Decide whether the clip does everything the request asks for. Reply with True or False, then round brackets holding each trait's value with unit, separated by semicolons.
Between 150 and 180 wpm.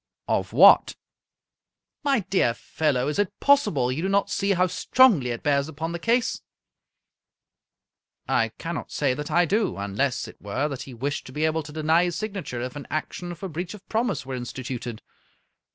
False (190 wpm)